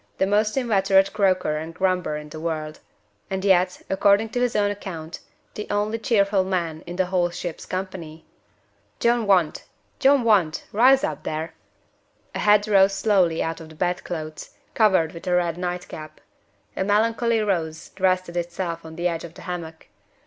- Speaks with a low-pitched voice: No, medium, 185 Hz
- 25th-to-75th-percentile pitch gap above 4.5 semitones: No, average, 3.7 semitones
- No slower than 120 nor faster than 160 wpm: No, average, 170 wpm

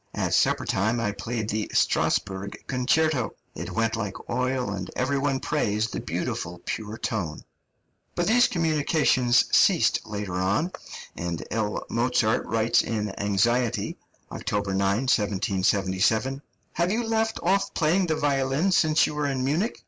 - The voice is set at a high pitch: No, low, 120 Hz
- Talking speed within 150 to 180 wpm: No, average, 140 wpm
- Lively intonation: Yes, wide, 6.5 semitones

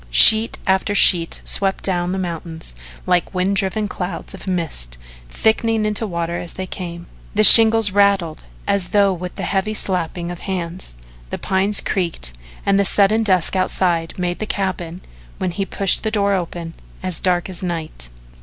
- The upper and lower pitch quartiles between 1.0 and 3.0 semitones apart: Yes, narrow, 2.6 semitones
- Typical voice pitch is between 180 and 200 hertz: Yes, medium, 185 Hz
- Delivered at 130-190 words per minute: Yes, average, 165 wpm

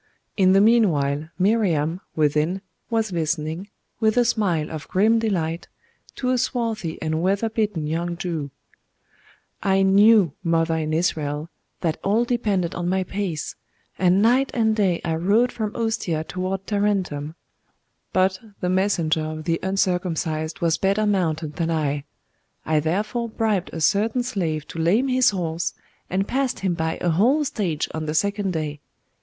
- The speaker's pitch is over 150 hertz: Yes, medium, 185 Hz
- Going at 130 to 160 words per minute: Yes, average, 150 wpm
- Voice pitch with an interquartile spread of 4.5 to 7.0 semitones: Yes, average, 4.8 semitones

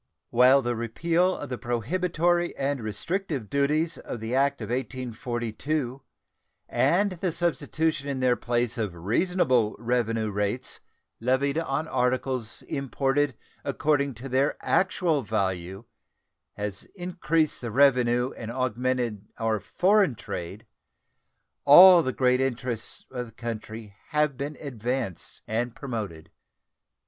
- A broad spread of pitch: No, average, 4.3 semitones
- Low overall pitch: Yes, low, 130 Hz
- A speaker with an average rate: No, slow, 120 wpm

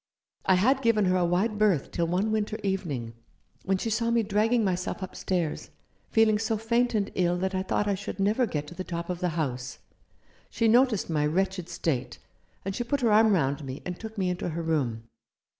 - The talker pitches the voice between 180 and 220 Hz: Yes, high, 190 Hz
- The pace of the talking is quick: Yes, fast, 210 wpm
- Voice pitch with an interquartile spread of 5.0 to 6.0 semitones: No, average, 4.3 semitones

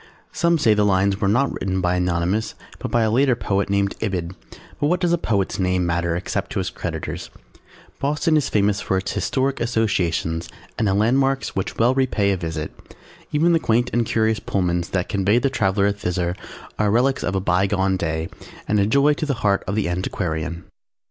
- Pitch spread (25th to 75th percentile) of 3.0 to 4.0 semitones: No, average, 4.6 semitones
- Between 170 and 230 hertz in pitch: No, low, 100 Hz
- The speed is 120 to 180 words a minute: No, average, 195 wpm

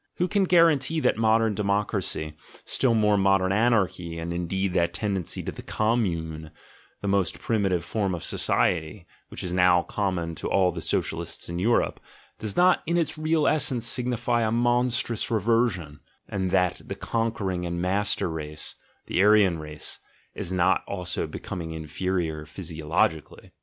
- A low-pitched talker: Yes, very low, 95 Hz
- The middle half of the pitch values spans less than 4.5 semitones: No, average, 4.9 semitones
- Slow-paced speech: No, average, 155 wpm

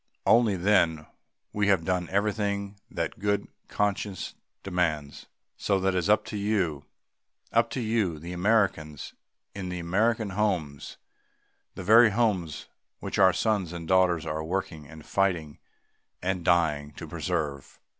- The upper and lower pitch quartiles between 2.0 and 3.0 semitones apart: No, average, 3.9 semitones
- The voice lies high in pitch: No, very low, 95 Hz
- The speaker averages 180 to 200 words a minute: No, slow, 135 wpm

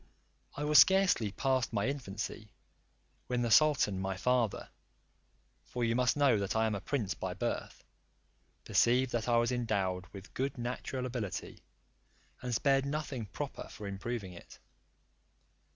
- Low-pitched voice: Yes, low, 120 Hz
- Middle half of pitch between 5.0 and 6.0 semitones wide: No, average, 4.3 semitones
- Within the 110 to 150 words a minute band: Yes, average, 140 wpm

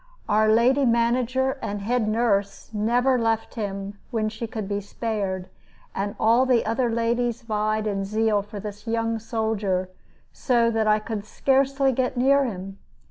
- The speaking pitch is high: Yes, high, 225 Hz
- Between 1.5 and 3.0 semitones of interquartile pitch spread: Yes, average, 2.7 semitones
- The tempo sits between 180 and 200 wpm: No, average, 155 wpm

